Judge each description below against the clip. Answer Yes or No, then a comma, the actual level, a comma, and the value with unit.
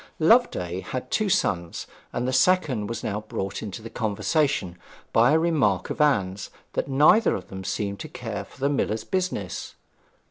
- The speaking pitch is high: No, low, 115 Hz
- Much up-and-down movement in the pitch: Yes, wide, 7.4 semitones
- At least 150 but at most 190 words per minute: Yes, average, 170 wpm